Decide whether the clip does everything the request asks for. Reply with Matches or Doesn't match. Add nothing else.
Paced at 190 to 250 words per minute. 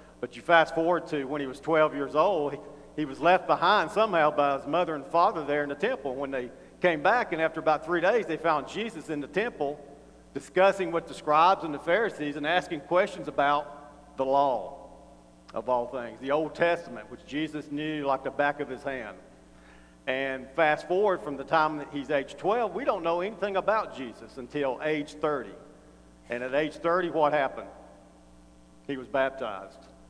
Matches